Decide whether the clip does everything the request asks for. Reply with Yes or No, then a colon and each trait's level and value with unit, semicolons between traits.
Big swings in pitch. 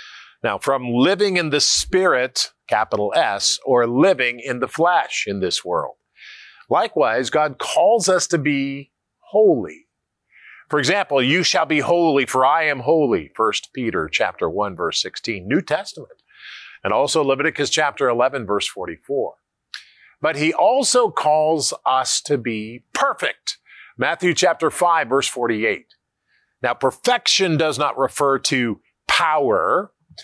Yes: wide, 5.9 semitones